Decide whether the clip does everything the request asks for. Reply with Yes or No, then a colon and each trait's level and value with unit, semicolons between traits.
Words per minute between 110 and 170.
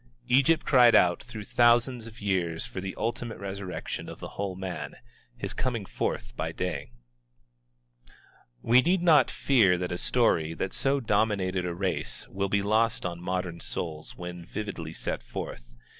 Yes: average, 160 wpm